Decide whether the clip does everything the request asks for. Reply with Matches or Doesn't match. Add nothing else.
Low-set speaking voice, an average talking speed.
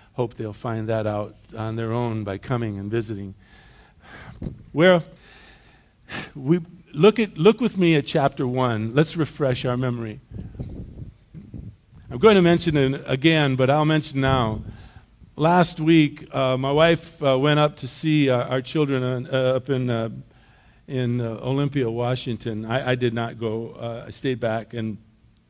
Matches